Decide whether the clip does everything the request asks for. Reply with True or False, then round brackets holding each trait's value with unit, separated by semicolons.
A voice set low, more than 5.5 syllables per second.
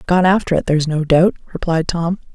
False (170 Hz; 5.8 syllables/s)